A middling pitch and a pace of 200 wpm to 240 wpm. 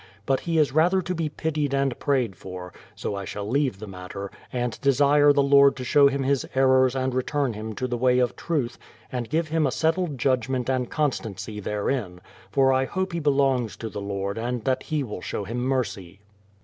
No: low, 130 Hz; fast, 205 wpm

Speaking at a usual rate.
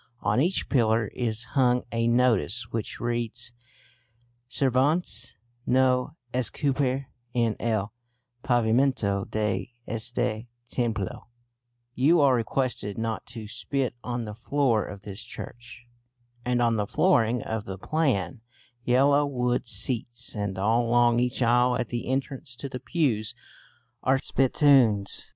No: slow, 125 wpm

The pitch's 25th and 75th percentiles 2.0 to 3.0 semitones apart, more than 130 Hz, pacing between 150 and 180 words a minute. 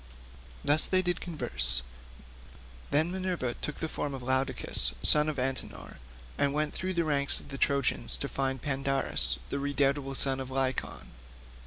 Yes: narrow, 2.4 semitones; medium, 140 Hz; average, 155 wpm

